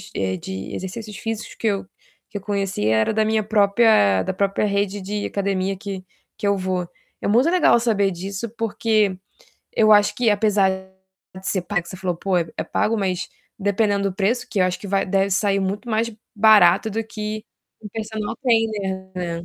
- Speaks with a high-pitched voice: Yes, high, 200 Hz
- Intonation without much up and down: Yes, narrow, 2.3 semitones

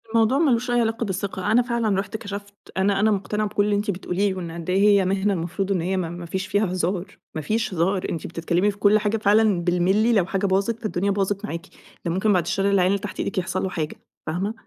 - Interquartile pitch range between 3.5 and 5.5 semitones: No, narrow, 2.5 semitones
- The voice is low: No, high, 195 Hz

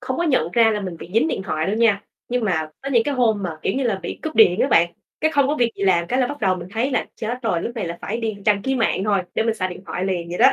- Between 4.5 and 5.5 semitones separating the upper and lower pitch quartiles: Yes, average, 5.1 semitones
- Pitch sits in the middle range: No, high, 220 Hz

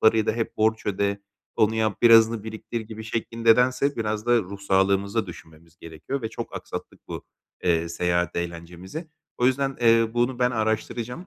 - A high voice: No, low, 110 Hz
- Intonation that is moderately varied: Yes, average, 3.4 semitones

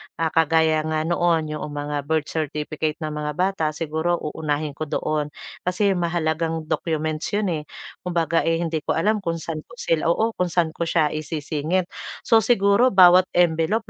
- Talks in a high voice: No, medium, 165 Hz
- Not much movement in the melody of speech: Yes, narrow, 2.3 semitones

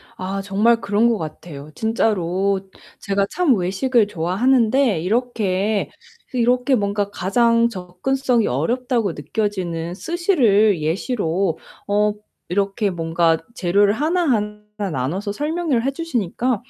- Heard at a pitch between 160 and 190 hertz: No, high, 205 Hz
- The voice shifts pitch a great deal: No, average, 4.7 semitones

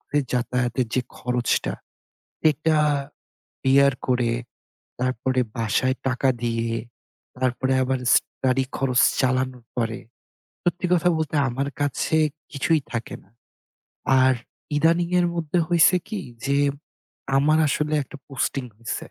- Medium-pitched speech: No, low, 130 Hz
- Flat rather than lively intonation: No, average, 3.3 semitones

